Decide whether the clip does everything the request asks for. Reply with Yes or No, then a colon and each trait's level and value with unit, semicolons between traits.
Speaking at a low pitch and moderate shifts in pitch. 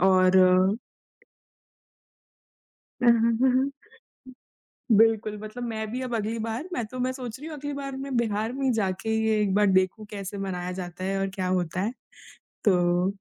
No: high, 215 Hz; average, 4.5 semitones